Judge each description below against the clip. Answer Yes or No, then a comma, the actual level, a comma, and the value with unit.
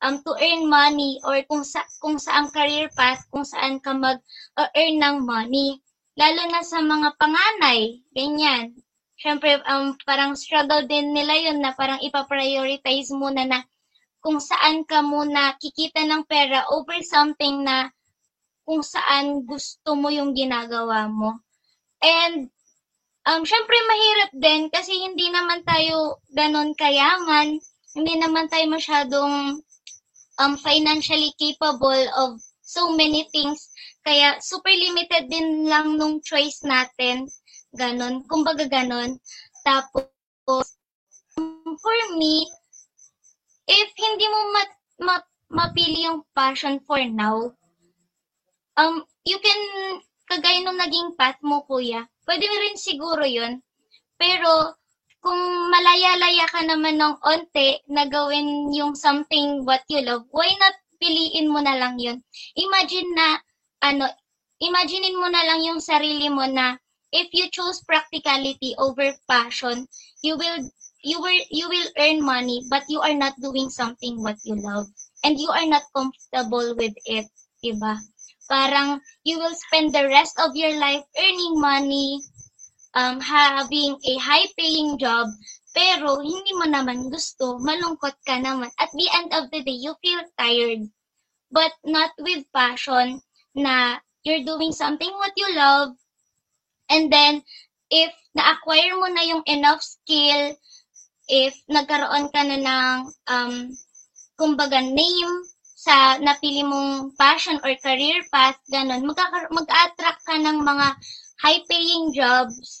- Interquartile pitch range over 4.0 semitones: No, average, 3.3 semitones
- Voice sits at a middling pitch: No, very high, 295 Hz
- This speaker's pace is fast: No, average, 135 wpm